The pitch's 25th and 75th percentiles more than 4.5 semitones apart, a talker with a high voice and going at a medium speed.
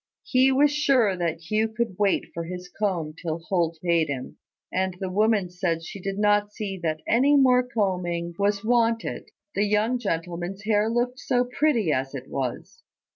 Yes: average, 5.1 semitones; high, 200 Hz; average, 175 wpm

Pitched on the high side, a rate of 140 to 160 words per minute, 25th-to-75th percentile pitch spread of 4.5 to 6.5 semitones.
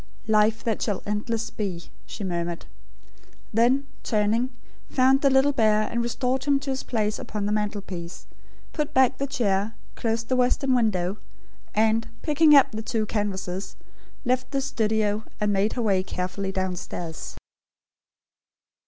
No: high, 220 Hz; average, 145 wpm; average, 4.0 semitones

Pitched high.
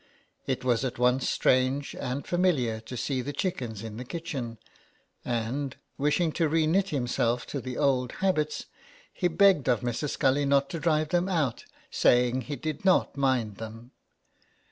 No: low, 135 Hz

